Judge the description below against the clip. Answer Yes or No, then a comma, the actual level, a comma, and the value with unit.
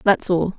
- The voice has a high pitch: No, medium, 175 Hz